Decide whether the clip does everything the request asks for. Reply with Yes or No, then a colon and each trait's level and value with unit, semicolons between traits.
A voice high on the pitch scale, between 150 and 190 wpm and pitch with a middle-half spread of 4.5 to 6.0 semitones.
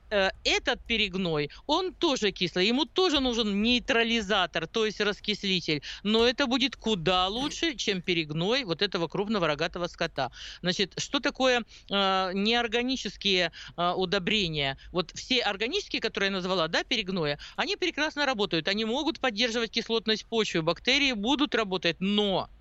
No: high, 210 Hz; average, 135 wpm; average, 5.3 semitones